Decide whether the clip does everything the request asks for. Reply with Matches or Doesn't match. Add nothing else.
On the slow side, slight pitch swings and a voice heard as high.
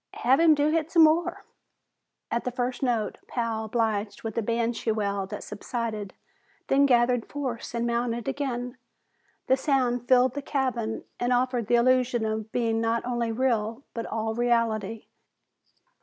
Doesn't match